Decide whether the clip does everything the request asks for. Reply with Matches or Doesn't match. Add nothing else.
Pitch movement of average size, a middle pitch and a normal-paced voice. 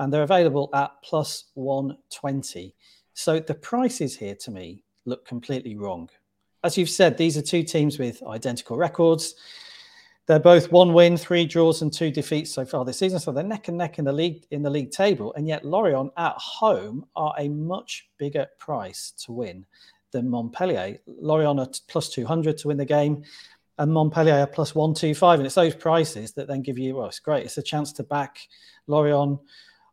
Matches